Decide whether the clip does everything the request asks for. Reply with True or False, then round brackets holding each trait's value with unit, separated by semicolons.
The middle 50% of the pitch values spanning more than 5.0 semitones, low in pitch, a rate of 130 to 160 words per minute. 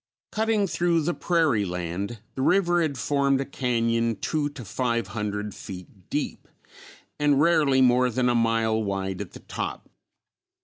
True (5.5 semitones; 125 Hz; 150 wpm)